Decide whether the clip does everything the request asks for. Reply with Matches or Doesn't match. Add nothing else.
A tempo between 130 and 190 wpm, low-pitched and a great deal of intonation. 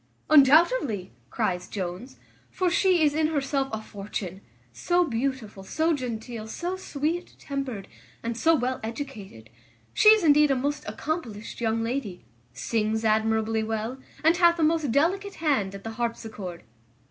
Doesn't match